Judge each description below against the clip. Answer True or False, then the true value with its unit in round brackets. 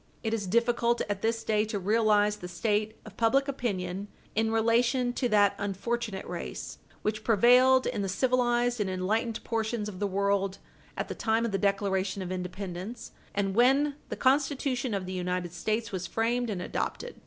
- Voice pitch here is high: True (215 Hz)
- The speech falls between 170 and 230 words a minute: True (175 wpm)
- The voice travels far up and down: False (3.4 semitones)